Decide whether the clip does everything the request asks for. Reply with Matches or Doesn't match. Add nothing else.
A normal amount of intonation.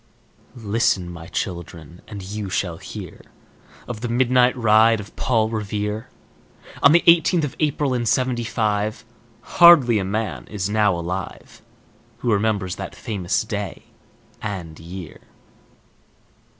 Matches